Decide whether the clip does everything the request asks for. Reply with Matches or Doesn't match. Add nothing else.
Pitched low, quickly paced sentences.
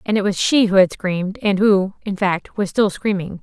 Doesn't match